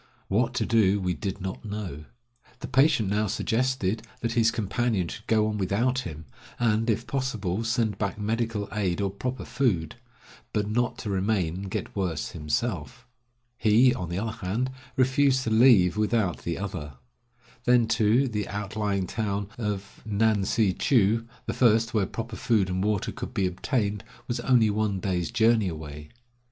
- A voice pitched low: Yes, low, 105 Hz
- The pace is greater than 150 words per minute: Yes, average, 165 wpm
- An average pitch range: Yes, average, 3.3 semitones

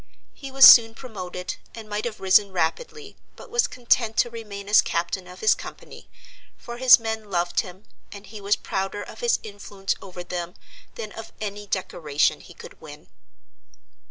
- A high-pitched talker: Yes, high, 205 Hz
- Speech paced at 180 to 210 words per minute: No, average, 170 wpm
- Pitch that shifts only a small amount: No, average, 3.5 semitones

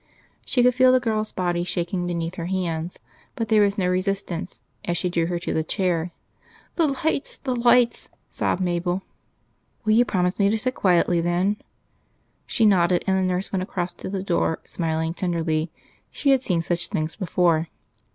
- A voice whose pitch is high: No, medium, 180 Hz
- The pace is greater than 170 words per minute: Yes, average, 180 wpm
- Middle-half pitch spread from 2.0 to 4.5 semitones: Yes, average, 3.4 semitones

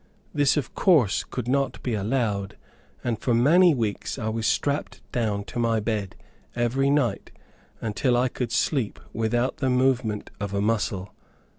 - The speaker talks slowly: No, average, 155 wpm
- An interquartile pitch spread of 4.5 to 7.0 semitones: No, average, 3.7 semitones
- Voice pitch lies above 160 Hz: No, low, 120 Hz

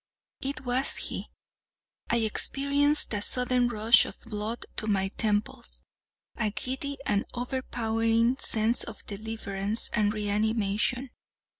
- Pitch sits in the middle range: No, high, 225 Hz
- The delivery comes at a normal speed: No, slow, 110 wpm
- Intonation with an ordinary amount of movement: Yes, average, 3.0 semitones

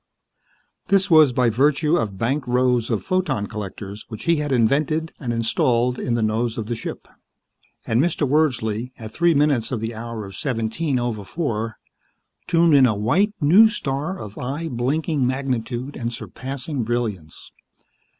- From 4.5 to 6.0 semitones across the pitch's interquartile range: Yes, average, 4.8 semitones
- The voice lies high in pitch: No, low, 125 Hz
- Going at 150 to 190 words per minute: Yes, average, 160 wpm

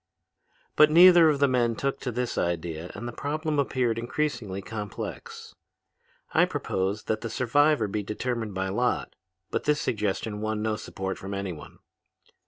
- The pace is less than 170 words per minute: Yes, average, 155 wpm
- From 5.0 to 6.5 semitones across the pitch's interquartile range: Yes, wide, 5.6 semitones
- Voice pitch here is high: No, low, 115 Hz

